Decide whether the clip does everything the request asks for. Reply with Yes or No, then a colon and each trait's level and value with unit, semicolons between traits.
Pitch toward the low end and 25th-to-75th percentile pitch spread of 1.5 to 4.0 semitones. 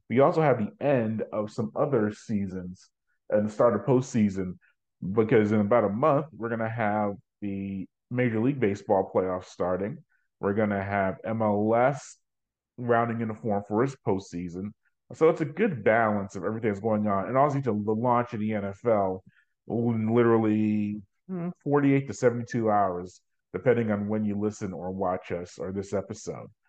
Yes: low, 110 Hz; average, 2.9 semitones